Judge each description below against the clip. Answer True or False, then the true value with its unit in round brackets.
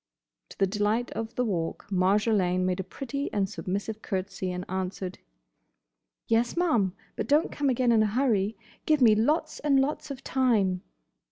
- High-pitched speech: True (215 Hz)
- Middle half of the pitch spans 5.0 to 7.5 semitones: True (5.5 semitones)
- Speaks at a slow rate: False (165 wpm)